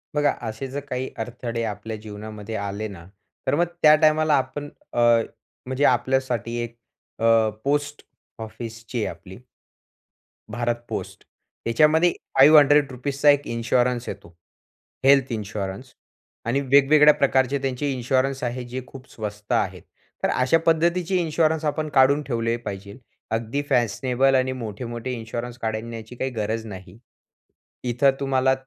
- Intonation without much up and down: No, average, 3.8 semitones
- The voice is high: No, low, 125 Hz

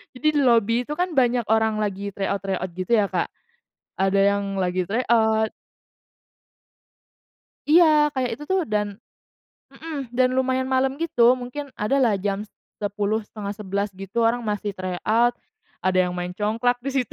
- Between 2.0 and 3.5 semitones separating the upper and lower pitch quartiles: No, average, 4.1 semitones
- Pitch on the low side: No, high, 220 Hz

